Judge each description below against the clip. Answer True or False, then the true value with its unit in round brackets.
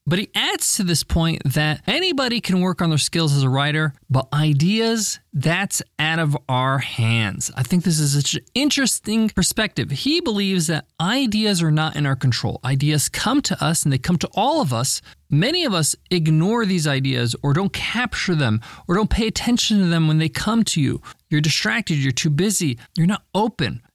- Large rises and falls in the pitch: True (6.5 semitones)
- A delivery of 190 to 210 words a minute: True (200 wpm)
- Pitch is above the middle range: False (165 Hz)